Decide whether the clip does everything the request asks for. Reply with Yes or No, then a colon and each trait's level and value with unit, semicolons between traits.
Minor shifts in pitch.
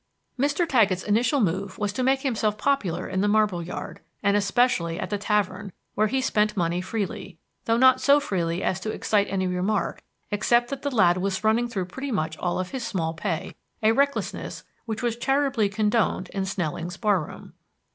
No: average, 4.5 semitones